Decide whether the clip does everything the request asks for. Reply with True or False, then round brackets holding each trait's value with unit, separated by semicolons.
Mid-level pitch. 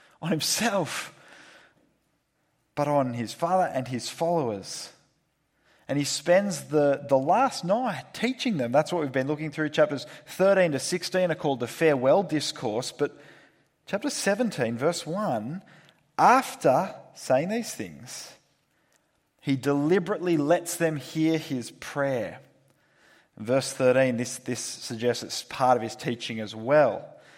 True (150 Hz)